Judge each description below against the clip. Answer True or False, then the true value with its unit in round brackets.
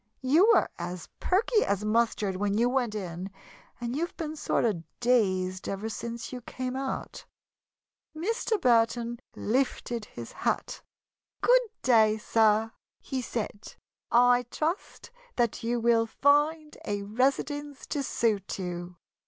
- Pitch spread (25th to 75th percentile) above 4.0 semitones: True (4.6 semitones)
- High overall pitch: True (235 Hz)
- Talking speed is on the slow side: True (130 wpm)